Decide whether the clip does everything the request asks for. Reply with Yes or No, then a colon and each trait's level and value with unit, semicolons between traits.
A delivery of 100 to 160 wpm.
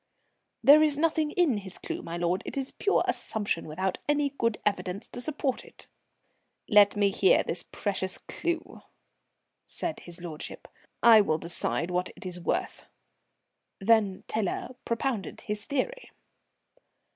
Yes: average, 140 wpm